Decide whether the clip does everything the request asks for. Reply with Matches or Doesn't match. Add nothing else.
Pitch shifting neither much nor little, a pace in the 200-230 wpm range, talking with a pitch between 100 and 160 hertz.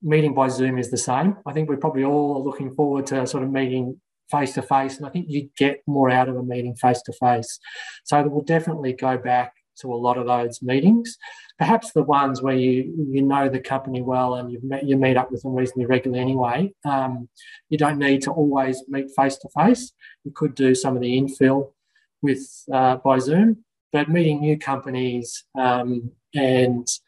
Doesn't match